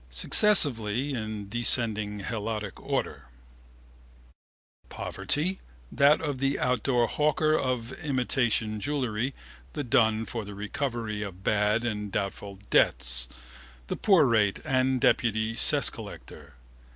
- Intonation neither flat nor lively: Yes, average, 4.3 semitones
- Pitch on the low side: Yes, low, 115 Hz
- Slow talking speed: Yes, slow, 110 wpm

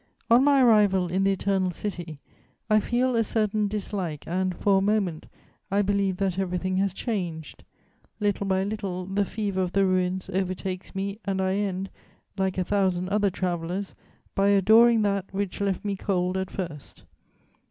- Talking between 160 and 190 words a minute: Yes, average, 165 wpm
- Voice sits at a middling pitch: No, high, 195 Hz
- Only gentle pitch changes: Yes, narrow, 1.7 semitones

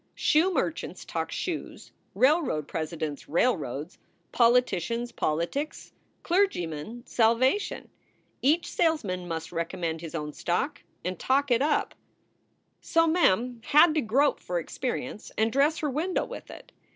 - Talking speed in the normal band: No, slow, 125 wpm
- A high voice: Yes, high, 240 Hz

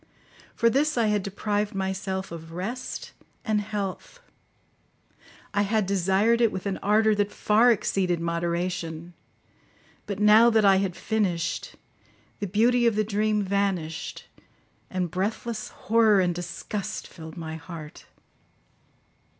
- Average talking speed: No, slow, 125 wpm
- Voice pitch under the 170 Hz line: No, high, 200 Hz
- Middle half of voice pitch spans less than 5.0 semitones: Yes, average, 3.2 semitones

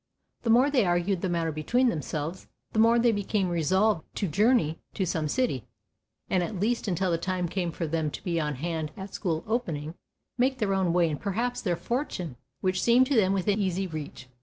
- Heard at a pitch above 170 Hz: Yes, medium, 185 Hz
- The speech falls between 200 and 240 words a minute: Yes, fast, 205 wpm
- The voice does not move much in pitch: No, average, 5.0 semitones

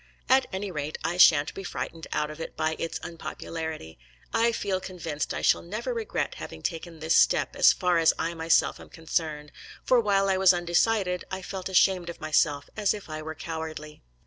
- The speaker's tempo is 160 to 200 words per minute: Yes, average, 195 wpm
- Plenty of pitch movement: No, average, 3.3 semitones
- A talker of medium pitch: Yes, medium, 170 Hz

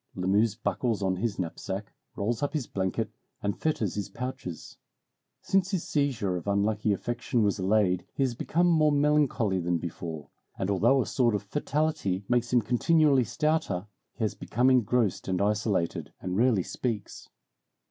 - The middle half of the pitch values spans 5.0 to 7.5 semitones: Yes, average, 5.3 semitones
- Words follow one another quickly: No, average, 155 wpm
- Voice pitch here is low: Yes, low, 110 Hz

